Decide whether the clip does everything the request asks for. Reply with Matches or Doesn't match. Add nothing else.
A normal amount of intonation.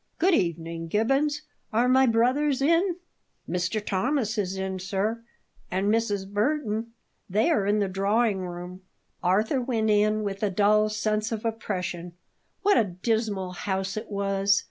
Matches